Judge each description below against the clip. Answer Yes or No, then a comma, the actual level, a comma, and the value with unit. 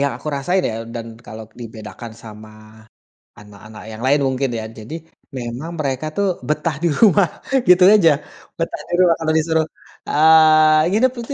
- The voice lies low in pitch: No, medium, 155 Hz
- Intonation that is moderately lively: No, wide, 6.0 semitones